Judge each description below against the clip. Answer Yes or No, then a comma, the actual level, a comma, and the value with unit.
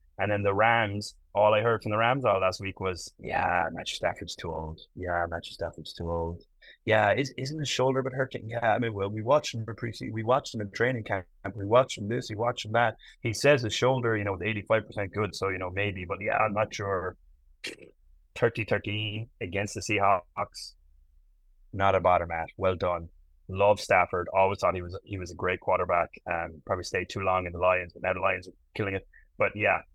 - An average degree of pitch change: Yes, average, 4.0 semitones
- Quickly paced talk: Yes, fast, 225 wpm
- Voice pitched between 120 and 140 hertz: No, low, 100 Hz